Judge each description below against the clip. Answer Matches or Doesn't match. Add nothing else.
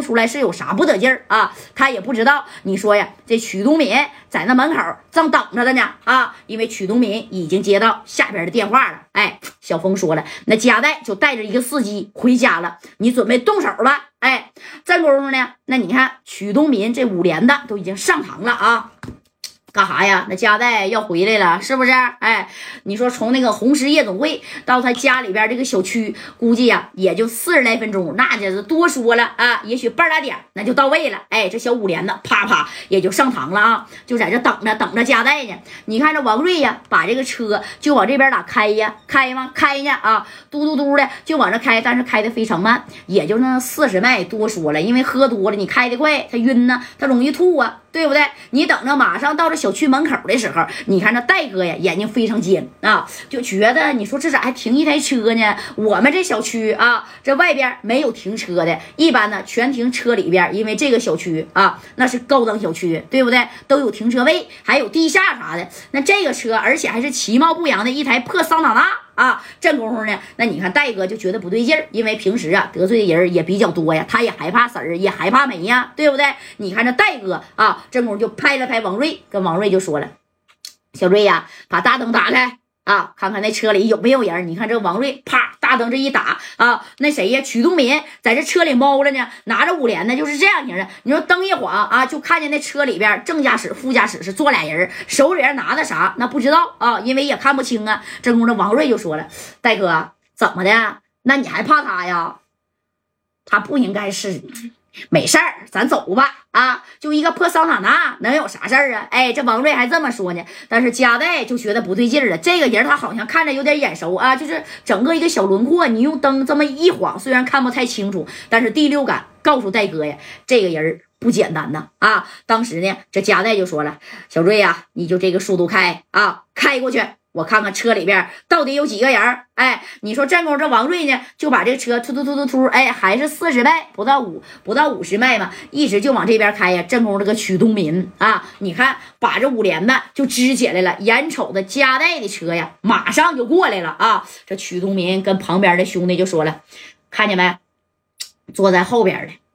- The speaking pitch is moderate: Doesn't match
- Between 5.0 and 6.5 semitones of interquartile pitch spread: Matches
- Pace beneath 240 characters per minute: Doesn't match